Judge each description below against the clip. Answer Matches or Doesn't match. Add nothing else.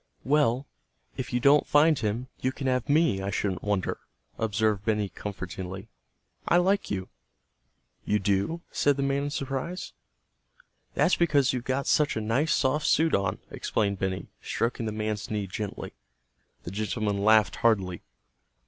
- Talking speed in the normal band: Matches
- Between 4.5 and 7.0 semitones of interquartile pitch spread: Matches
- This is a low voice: Matches